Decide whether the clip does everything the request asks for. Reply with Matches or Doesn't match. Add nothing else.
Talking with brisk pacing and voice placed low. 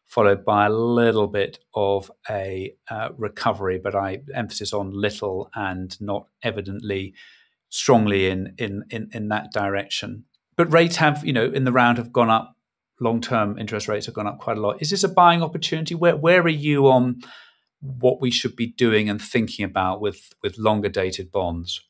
Doesn't match